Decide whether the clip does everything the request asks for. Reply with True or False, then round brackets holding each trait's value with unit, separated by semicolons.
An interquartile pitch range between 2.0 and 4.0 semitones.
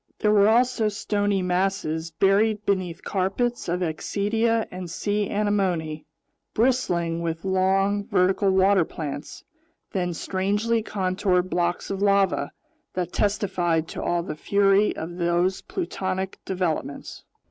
True (2.7 semitones)